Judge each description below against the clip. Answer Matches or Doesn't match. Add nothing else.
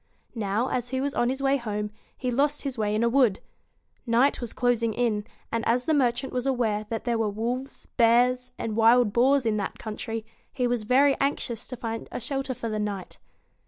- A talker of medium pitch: Doesn't match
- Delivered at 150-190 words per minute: Doesn't match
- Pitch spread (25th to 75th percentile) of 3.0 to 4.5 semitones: Doesn't match